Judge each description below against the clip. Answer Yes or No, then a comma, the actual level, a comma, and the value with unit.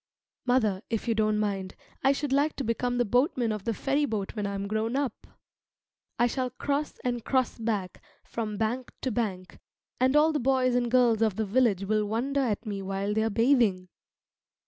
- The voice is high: Yes, high, 230 Hz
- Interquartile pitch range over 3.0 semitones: Yes, average, 3.5 semitones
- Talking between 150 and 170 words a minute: No, average, 190 wpm